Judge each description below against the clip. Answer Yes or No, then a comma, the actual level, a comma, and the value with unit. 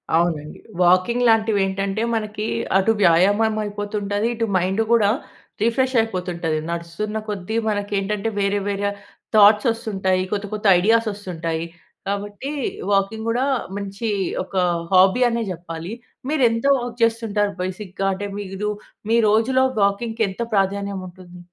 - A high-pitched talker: Yes, high, 205 Hz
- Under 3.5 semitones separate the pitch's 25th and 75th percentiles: Yes, average, 2.9 semitones